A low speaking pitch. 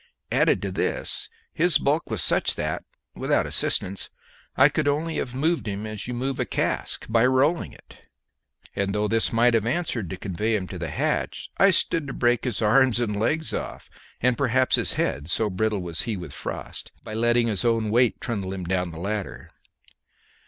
Yes: low, 115 Hz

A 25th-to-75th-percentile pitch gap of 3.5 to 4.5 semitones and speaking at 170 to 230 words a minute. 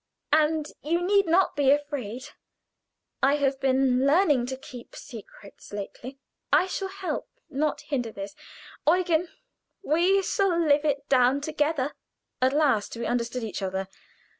No: average, 4.2 semitones; average, 140 wpm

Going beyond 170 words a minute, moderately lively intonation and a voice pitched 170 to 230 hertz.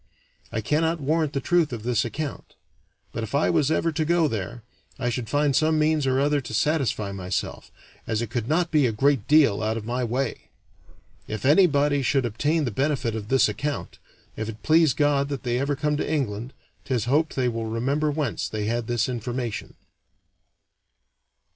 No: average, 185 wpm; average, 4.6 semitones; low, 135 Hz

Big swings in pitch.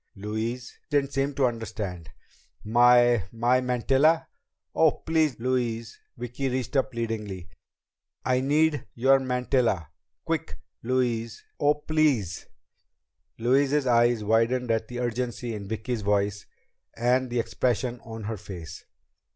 No: average, 2.8 semitones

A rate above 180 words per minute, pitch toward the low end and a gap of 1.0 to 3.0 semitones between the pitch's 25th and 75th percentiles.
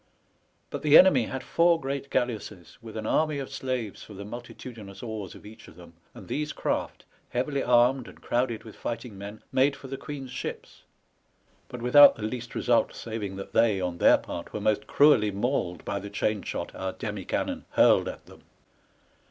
No: average, 190 wpm; low, 115 Hz; average, 4.3 semitones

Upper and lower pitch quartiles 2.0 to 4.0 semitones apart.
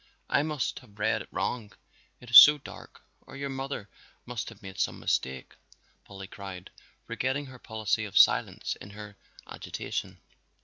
No: average, 4.9 semitones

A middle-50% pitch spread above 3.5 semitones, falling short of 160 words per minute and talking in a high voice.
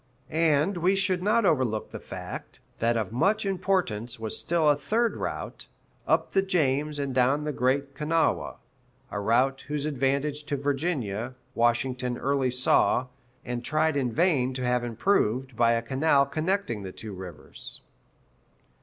No: average, 4.5 semitones; average, 150 wpm; low, 135 Hz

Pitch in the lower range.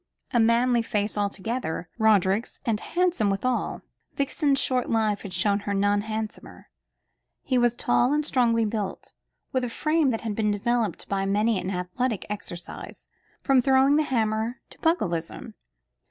No: high, 225 Hz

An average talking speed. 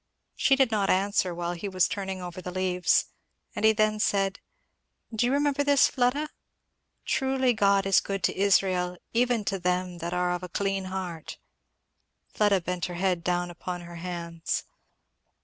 Yes: average, 165 wpm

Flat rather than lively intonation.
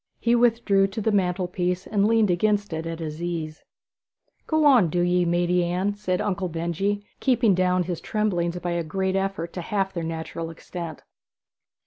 No: average, 3.0 semitones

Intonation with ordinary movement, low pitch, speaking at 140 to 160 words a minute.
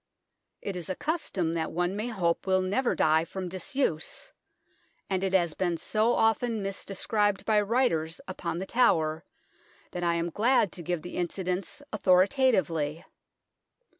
No: average, 4.1 semitones; medium, 185 Hz; average, 145 wpm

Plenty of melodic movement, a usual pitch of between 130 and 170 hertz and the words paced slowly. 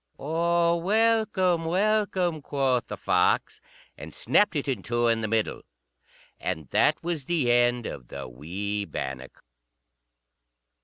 Yes: wide, 7.6 semitones; medium, 140 Hz; slow, 125 wpm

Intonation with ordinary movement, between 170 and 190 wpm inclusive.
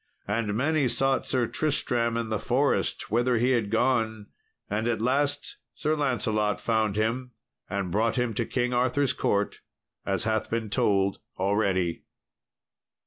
No: average, 3.2 semitones; average, 140 wpm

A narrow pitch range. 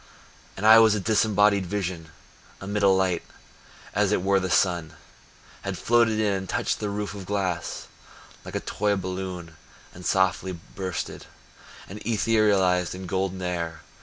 Yes: narrow, 2.2 semitones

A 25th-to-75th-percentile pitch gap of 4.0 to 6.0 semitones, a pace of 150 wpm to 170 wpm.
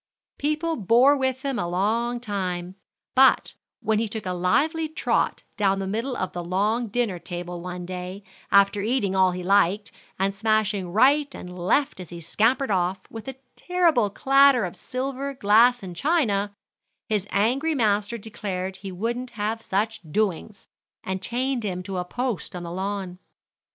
Yes: average, 4.9 semitones; average, 165 wpm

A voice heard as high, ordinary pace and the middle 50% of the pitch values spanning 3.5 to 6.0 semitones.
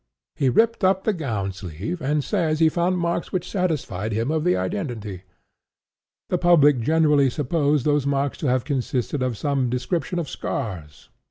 No: medium, 145 Hz; average, 165 wpm; wide, 5.6 semitones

